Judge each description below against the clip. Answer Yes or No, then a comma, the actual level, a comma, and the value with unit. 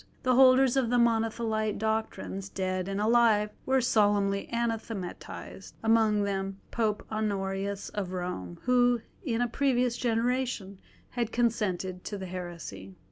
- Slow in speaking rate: Yes, slow, 125 wpm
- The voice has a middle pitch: No, high, 215 Hz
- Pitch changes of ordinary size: Yes, average, 3.5 semitones